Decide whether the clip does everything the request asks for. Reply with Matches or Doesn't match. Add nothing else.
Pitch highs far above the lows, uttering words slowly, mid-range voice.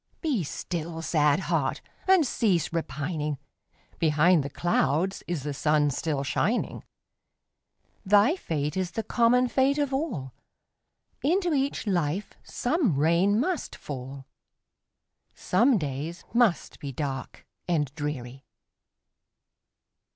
Matches